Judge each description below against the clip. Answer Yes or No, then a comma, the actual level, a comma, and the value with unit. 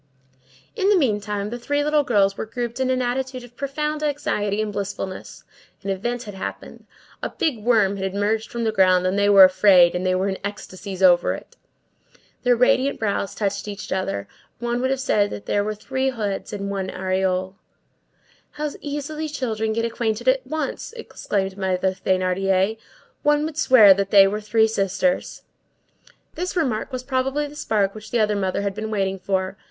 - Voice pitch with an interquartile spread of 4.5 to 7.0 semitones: Yes, average, 4.9 semitones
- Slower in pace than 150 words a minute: No, average, 180 wpm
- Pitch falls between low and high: No, high, 215 Hz